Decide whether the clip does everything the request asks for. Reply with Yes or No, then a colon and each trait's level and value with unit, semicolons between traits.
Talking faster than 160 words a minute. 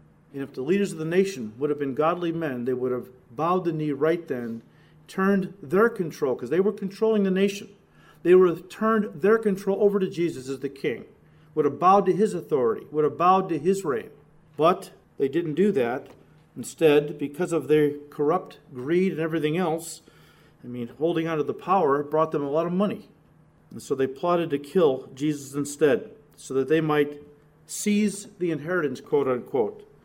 Yes: average, 190 wpm